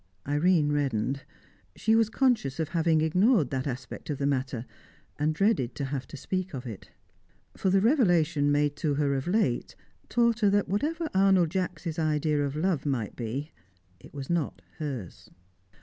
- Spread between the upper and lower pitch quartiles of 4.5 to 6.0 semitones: Yes, wide, 5.4 semitones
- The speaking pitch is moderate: Yes, medium, 155 Hz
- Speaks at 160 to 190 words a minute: Yes, average, 165 wpm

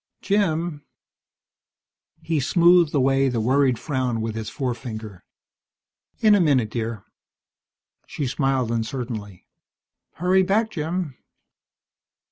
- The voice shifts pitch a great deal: Yes, wide, 6.4 semitones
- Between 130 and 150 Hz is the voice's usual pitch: Yes, low, 135 Hz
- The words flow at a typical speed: No, slow, 100 wpm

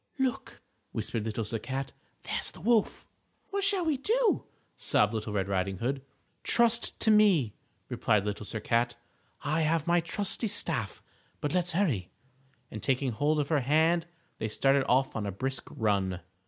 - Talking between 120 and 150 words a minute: No, average, 160 wpm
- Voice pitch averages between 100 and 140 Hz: Yes, low, 135 Hz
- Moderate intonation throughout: No, wide, 8.6 semitones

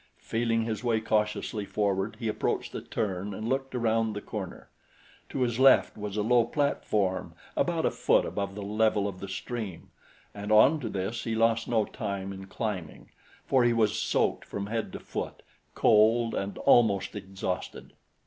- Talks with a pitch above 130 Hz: No, low, 110 Hz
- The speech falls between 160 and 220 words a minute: Yes, average, 170 wpm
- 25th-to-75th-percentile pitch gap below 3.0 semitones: Yes, narrow, 2.6 semitones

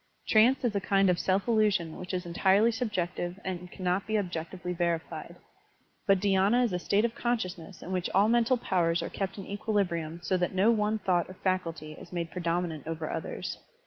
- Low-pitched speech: No, medium, 185 Hz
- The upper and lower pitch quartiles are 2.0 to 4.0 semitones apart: Yes, average, 3.2 semitones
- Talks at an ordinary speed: Yes, average, 190 wpm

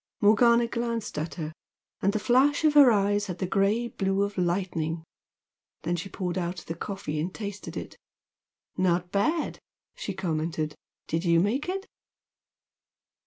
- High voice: Yes, high, 195 Hz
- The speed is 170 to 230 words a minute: No, average, 150 wpm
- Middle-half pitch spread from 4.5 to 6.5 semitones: Yes, average, 4.8 semitones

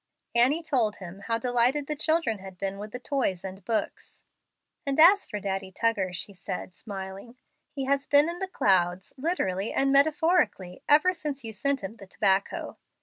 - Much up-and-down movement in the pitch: Yes, wide, 6.9 semitones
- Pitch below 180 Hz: No, high, 230 Hz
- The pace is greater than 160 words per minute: Yes, average, 175 wpm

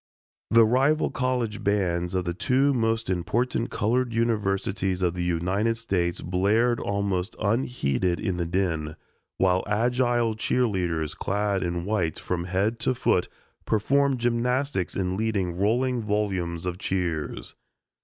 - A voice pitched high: No, low, 100 Hz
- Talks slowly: Yes, slow, 130 wpm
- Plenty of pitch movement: No, average, 4.6 semitones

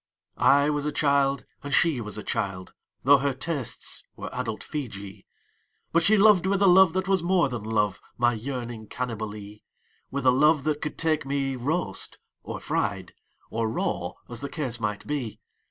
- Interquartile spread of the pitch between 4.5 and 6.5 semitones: Yes, wide, 5.4 semitones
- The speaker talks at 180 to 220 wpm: Yes, average, 185 wpm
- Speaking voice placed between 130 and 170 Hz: Yes, medium, 140 Hz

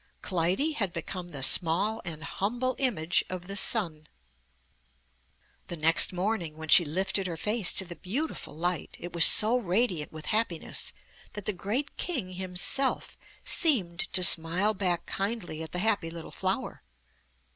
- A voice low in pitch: No, medium, 185 Hz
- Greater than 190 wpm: No, average, 150 wpm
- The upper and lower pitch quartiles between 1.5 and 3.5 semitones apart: No, average, 4.3 semitones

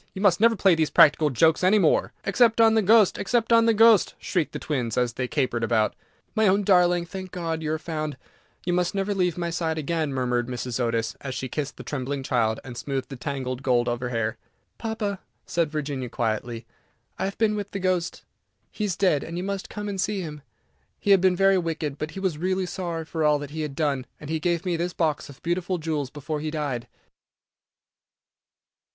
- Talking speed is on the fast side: Yes, fast, 215 wpm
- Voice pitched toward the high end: No, medium, 160 Hz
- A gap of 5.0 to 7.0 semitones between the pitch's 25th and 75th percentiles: Yes, wide, 5.6 semitones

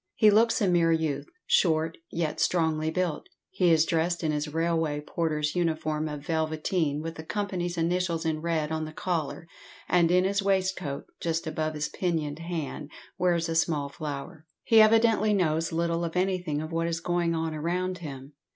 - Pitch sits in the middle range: Yes, medium, 165 Hz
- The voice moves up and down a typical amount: No, narrow, 2.3 semitones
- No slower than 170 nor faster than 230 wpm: Yes, average, 175 wpm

